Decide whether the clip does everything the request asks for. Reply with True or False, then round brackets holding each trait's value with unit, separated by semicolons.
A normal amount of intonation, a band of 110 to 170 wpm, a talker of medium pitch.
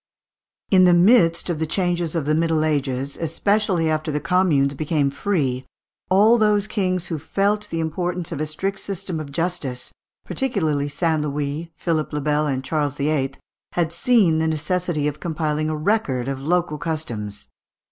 True (3.4 semitones; 165 wpm; 160 Hz)